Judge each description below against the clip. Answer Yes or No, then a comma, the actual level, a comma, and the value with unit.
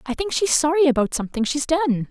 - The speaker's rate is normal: No, fast, 230 wpm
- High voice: Yes, very high, 285 Hz